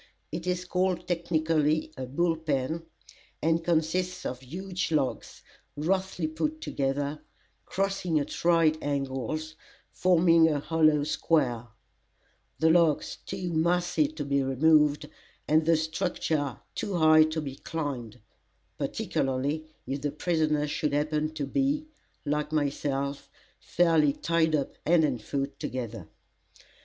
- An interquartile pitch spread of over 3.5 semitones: No, average, 2.9 semitones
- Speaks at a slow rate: Yes, slow, 125 wpm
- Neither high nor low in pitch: Yes, medium, 155 Hz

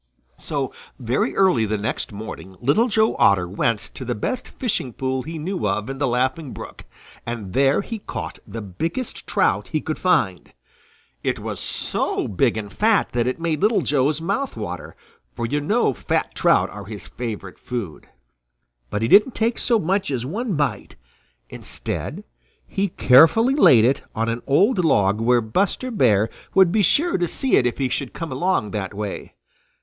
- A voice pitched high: No, low, 135 Hz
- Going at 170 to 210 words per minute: Yes, average, 175 wpm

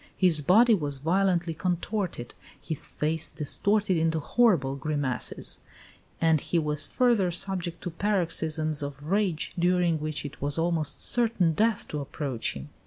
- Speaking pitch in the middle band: Yes, medium, 165 Hz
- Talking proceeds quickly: No, average, 140 wpm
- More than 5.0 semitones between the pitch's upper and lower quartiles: No, average, 3.9 semitones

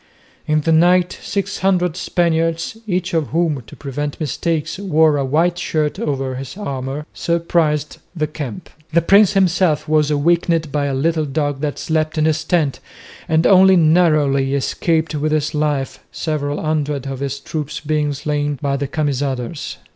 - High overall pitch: No, medium, 155 Hz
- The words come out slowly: No, average, 160 wpm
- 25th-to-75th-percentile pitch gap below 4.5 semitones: Yes, narrow, 2.6 semitones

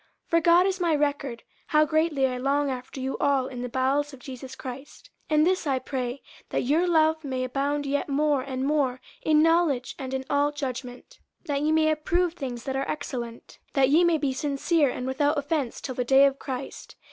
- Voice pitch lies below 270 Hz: No, very high, 280 Hz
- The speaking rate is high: Yes, fast, 215 wpm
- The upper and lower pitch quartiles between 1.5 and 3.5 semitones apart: Yes, average, 2.8 semitones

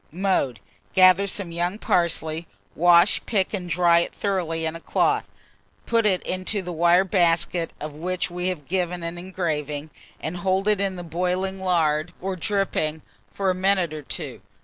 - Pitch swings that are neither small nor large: No, narrow, 2.2 semitones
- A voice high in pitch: No, medium, 180 Hz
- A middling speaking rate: Yes, average, 165 wpm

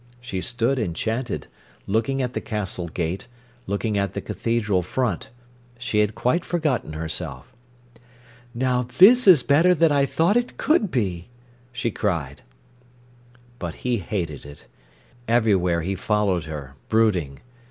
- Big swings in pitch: Yes, wide, 6.4 semitones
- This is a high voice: No, low, 105 Hz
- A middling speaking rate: No, slow, 130 wpm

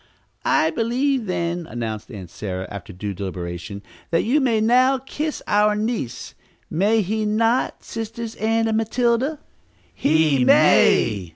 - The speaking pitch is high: Yes, high, 210 Hz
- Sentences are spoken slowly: Yes, slow, 130 wpm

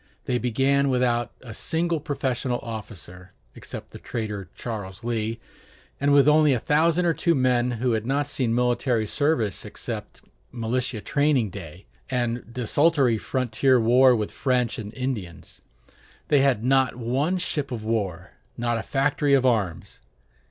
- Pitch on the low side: Yes, low, 125 Hz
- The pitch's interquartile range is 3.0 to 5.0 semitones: Yes, average, 3.7 semitones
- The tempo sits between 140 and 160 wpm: Yes, average, 145 wpm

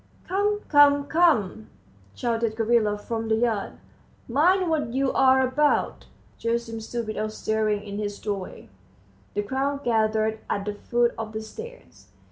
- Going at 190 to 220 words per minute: No, slow, 135 wpm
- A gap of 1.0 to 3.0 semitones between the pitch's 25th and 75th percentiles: No, average, 4.5 semitones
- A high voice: Yes, high, 230 Hz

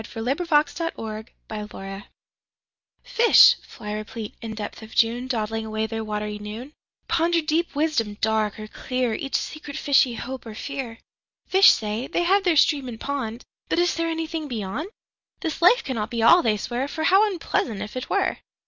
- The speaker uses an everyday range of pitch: No, wide, 6.5 semitones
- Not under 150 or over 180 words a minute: Yes, average, 155 wpm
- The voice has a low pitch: No, very high, 250 Hz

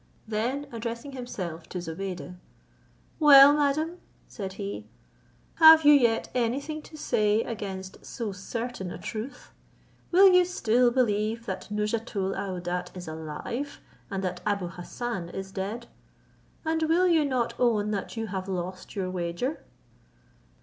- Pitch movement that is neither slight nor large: No, wide, 6.0 semitones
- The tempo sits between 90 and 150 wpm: Yes, slow, 135 wpm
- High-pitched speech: Yes, high, 220 Hz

